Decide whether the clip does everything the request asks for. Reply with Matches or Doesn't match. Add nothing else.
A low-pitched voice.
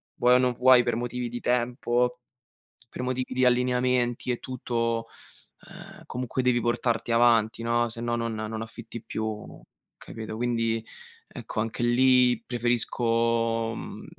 Matches